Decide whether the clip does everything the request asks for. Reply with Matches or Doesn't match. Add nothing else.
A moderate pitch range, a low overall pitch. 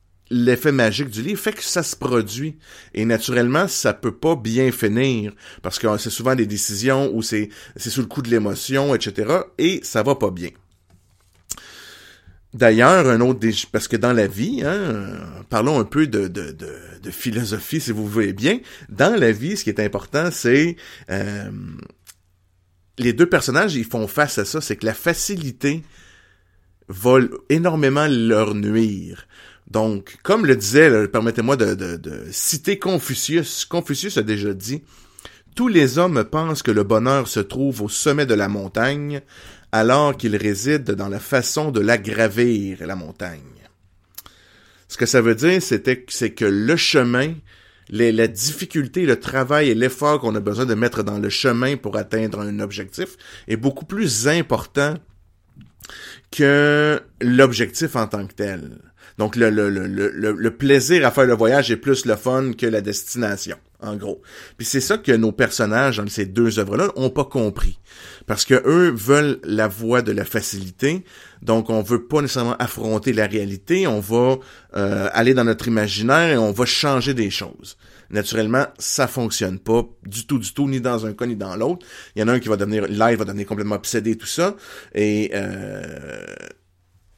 Matches